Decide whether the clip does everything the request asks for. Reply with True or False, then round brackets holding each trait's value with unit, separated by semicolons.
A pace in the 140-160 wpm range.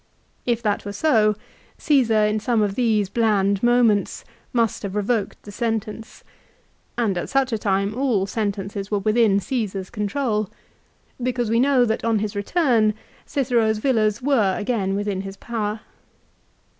True (150 wpm)